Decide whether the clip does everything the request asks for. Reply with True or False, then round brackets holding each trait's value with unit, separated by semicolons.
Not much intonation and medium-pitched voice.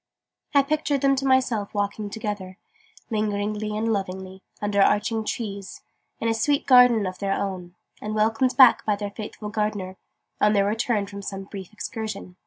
False (2.1 semitones; 210 Hz)